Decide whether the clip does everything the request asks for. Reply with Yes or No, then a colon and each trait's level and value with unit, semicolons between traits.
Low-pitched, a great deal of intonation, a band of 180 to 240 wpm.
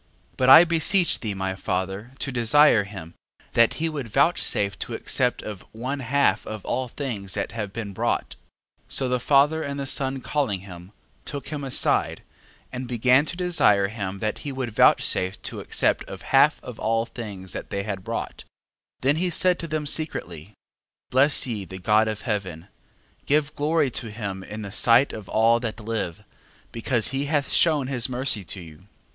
Yes: low, 115 Hz; wide, 5.8 semitones; average, 185 wpm